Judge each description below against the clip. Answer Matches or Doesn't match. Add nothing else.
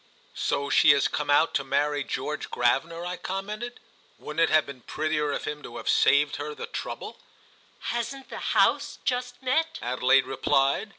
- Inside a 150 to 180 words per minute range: Matches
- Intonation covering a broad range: Matches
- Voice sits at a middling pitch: Matches